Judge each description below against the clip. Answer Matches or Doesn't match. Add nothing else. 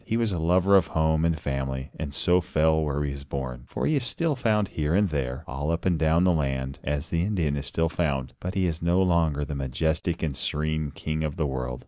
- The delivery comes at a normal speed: Doesn't match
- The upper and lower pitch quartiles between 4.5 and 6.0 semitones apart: Doesn't match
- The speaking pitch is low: Matches